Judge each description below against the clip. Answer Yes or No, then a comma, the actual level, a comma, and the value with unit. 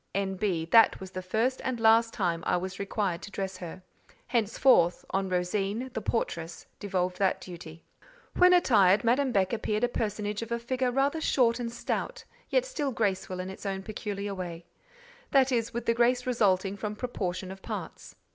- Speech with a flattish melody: No, average, 4.2 semitones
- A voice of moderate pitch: No, high, 205 Hz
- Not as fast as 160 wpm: No, average, 175 wpm